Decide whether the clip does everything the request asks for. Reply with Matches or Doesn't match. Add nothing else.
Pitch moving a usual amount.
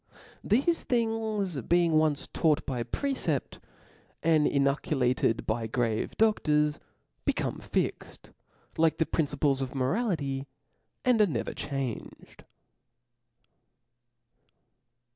Doesn't match